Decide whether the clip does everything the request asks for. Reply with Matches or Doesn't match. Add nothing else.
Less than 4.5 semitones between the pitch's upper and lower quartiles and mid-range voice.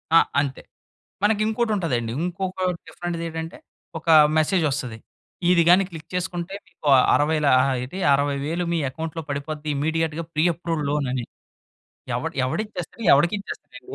Matches